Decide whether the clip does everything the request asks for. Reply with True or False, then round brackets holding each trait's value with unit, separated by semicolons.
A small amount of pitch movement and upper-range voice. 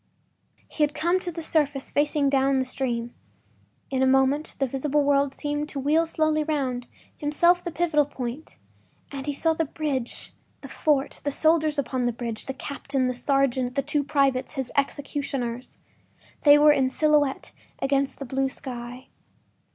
True (2.2 semitones; 280 Hz)